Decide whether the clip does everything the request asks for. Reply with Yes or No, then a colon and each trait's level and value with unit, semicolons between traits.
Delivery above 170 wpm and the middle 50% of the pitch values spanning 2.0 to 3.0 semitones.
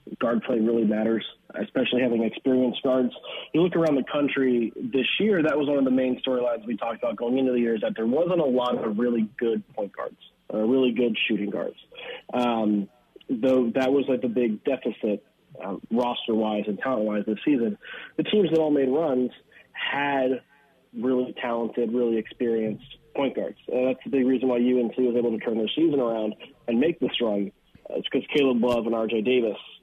Yes: average, 195 wpm; narrow, 2.5 semitones